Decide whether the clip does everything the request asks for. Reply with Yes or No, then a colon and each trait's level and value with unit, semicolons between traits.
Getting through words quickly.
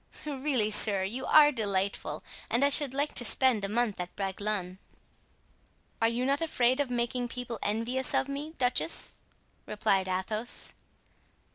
No: average, 145 wpm